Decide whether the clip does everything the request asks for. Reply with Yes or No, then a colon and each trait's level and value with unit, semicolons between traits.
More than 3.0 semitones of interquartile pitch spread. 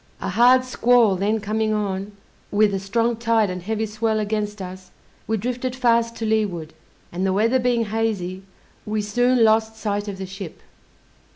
No: average, 2.7 semitones